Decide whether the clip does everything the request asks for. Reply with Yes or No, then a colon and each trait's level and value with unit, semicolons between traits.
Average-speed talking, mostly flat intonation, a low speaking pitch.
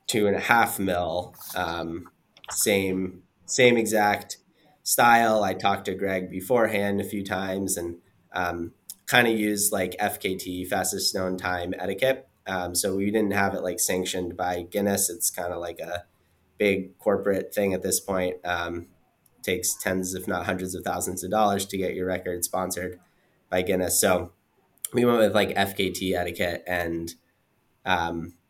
Yes: average, 160 wpm; narrow, 2.0 semitones; very low, 95 Hz